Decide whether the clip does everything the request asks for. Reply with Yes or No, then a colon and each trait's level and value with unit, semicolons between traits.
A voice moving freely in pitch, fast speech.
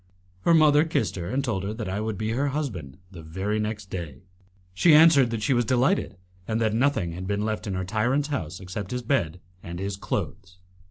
Yes: wide, 6.0 semitones; fast, 215 wpm